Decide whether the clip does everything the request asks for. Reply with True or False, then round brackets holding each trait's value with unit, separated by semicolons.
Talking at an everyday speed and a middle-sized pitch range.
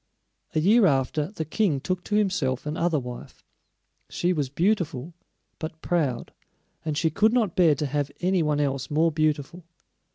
True (160 wpm; 3.8 semitones)